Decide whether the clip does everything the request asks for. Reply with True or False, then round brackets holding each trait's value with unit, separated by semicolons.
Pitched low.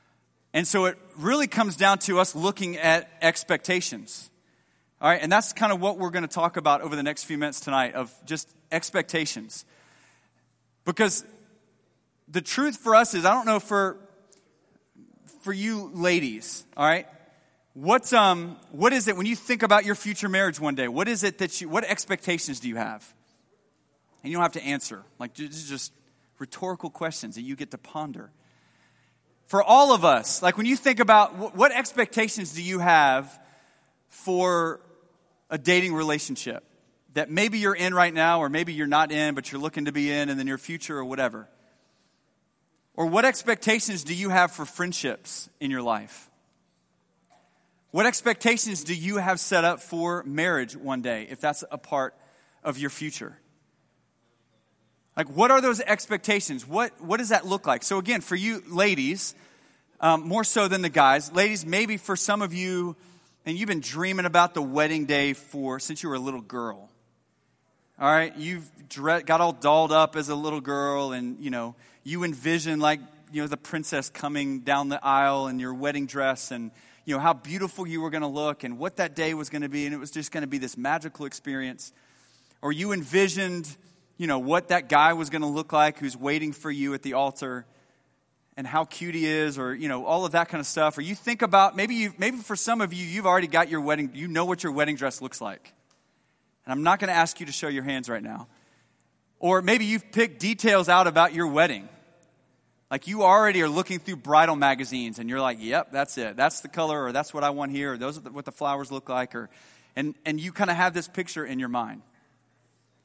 False (160 Hz)